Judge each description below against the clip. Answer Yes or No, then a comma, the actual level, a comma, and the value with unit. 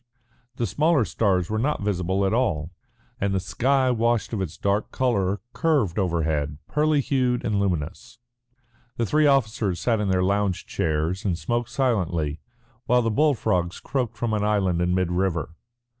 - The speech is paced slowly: No, average, 165 wpm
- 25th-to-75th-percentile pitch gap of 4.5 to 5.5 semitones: Yes, average, 5.1 semitones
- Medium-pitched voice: No, low, 100 Hz